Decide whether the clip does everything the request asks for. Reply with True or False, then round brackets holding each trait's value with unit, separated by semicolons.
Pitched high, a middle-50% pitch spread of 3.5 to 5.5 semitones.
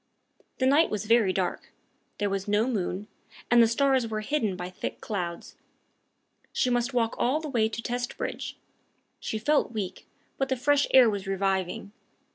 True (225 Hz; 4.5 semitones)